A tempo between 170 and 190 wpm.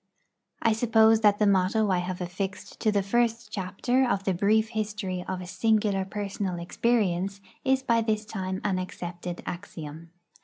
No: average, 160 wpm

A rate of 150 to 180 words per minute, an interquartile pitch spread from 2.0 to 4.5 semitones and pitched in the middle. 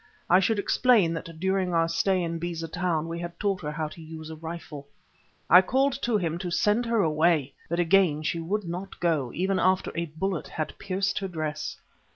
No: average, 200 wpm; average, 2.9 semitones; medium, 170 Hz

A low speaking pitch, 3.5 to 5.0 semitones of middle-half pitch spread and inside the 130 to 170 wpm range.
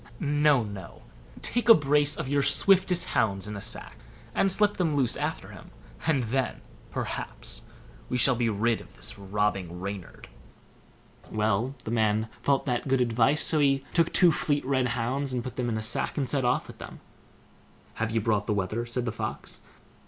No: low, 125 Hz; average, 4.7 semitones; average, 180 wpm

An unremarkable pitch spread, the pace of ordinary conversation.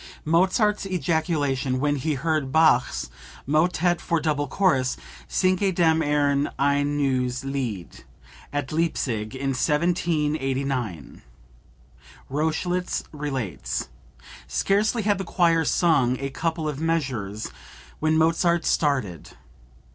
No: average, 3.9 semitones; slow, 100 wpm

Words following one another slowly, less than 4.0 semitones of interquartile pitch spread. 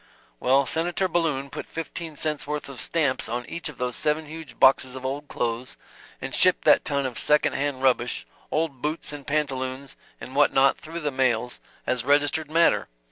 No: average, 185 wpm; average, 2.8 semitones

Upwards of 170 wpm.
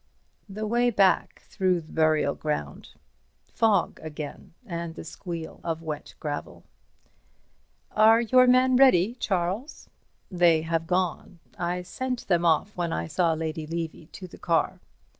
No: average, 140 wpm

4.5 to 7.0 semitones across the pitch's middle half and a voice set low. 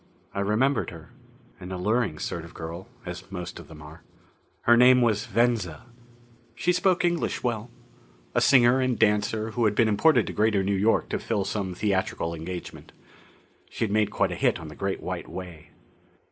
Yes: average, 4.8 semitones; low, 105 Hz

